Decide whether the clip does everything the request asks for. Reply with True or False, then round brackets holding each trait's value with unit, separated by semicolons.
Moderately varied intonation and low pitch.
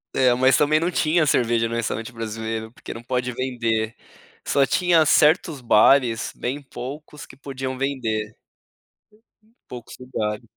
True (3.7 semitones; 125 Hz)